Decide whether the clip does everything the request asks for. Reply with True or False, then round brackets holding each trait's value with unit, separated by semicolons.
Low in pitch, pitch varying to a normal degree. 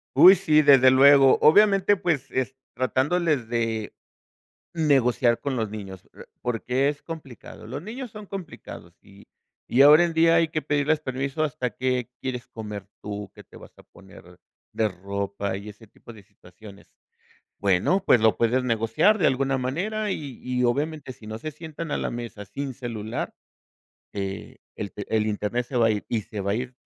False (125 Hz; 5.8 semitones)